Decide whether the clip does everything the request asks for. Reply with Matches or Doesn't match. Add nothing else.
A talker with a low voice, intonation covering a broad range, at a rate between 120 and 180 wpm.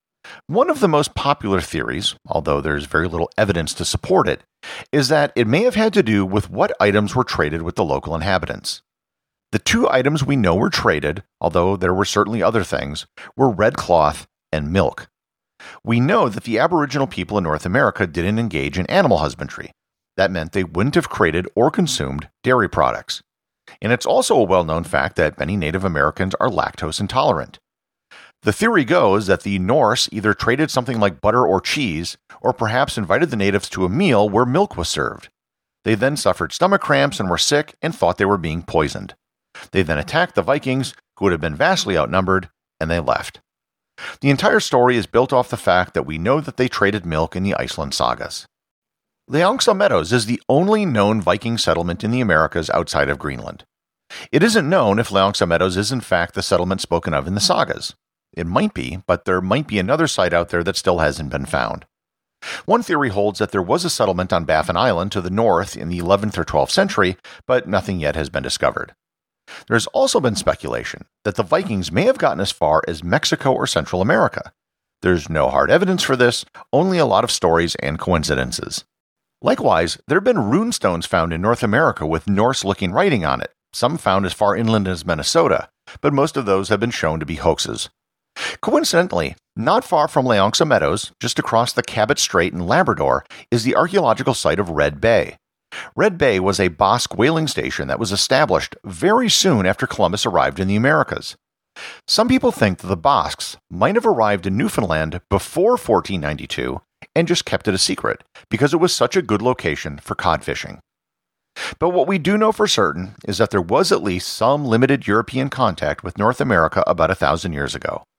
Doesn't match